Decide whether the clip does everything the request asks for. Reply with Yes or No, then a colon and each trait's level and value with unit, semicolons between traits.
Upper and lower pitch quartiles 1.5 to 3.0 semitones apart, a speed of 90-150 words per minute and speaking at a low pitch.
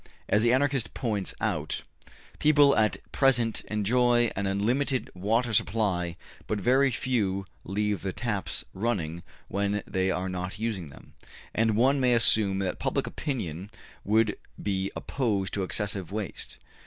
No: average, 3.8 semitones; average, 140 wpm; low, 105 Hz